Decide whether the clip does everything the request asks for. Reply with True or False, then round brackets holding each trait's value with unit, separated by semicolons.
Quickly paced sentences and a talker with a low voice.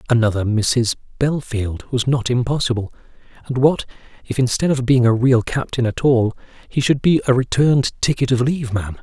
False (175 wpm; 125 Hz)